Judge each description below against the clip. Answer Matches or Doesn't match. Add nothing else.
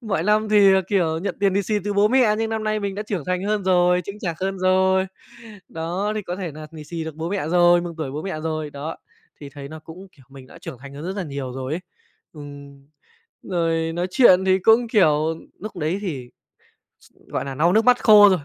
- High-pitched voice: Doesn't match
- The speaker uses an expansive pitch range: Doesn't match